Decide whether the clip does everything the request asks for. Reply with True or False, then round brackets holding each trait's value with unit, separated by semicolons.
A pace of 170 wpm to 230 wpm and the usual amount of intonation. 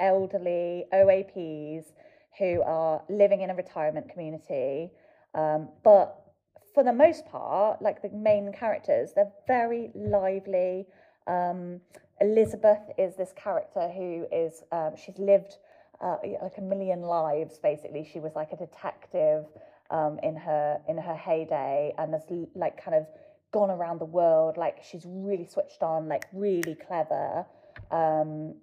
False (140 wpm; 4.1 semitones)